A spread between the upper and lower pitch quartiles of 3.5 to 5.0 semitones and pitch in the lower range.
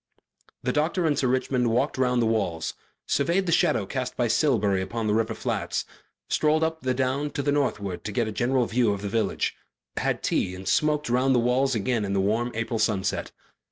Yes: average, 4.1 semitones; low, 125 Hz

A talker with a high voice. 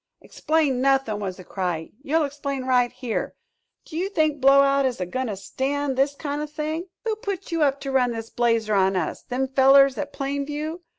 Yes: very high, 275 Hz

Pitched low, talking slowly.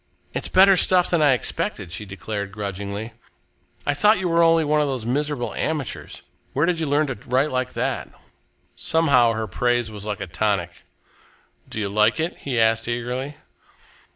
No: low, 125 Hz; average, 175 wpm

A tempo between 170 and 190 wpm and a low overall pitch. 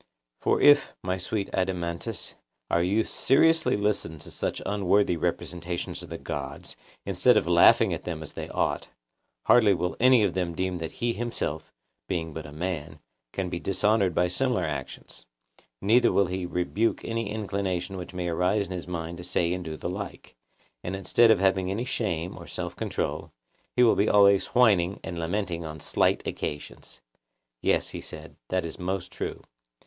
Yes: average, 175 wpm; very low, 90 Hz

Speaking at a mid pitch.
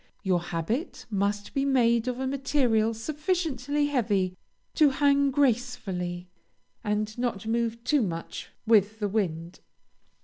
No: high, 230 Hz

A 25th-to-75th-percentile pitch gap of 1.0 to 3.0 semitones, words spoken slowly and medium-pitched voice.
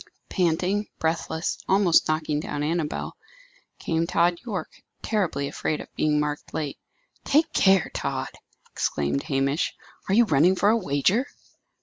No: average, 4.4 semitones; slow, 130 wpm; medium, 160 Hz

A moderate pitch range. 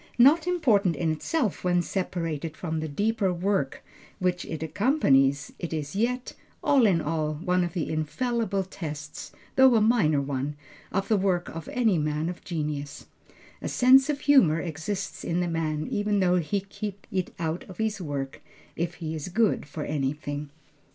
Yes: average, 5.0 semitones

